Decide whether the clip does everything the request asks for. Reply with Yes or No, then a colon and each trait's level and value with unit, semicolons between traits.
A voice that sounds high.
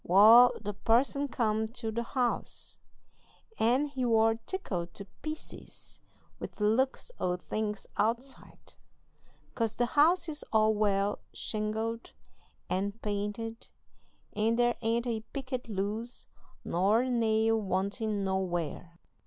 Yes: high, 225 Hz